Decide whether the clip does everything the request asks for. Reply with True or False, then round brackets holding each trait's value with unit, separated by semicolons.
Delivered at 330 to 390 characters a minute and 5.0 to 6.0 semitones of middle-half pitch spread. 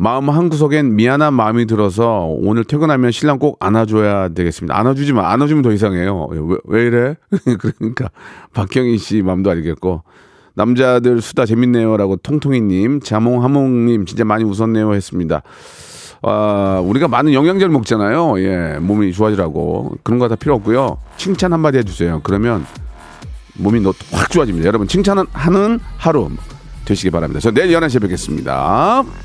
True (360 characters per minute; 5.6 semitones)